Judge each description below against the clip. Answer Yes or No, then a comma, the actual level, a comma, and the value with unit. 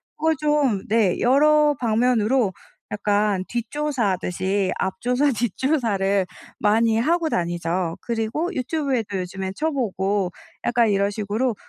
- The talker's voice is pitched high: Yes, high, 225 Hz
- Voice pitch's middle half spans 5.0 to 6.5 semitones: Yes, average, 5.3 semitones